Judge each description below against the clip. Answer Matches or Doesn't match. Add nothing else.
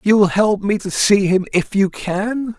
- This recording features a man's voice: Matches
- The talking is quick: Matches